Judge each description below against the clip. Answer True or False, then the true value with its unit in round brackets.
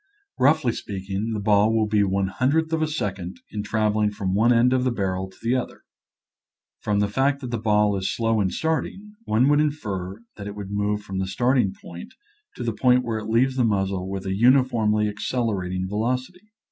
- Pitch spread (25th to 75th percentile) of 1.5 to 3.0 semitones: False (4.2 semitones)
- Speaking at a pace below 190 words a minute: False (205 wpm)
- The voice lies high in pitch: False (110 Hz)